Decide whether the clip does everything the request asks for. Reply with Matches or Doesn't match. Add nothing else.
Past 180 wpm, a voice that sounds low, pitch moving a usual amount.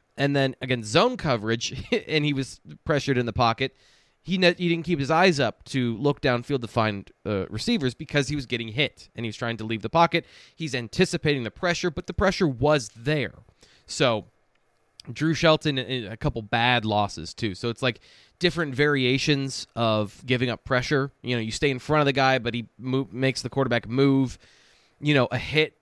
Matches